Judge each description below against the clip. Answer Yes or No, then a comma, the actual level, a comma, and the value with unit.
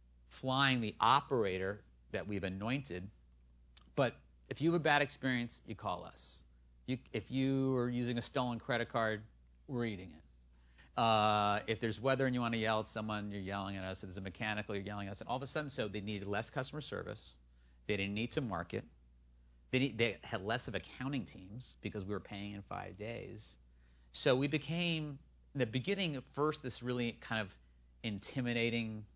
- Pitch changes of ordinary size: No, wide, 6.4 semitones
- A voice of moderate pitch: No, low, 105 Hz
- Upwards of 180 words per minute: Yes, average, 195 wpm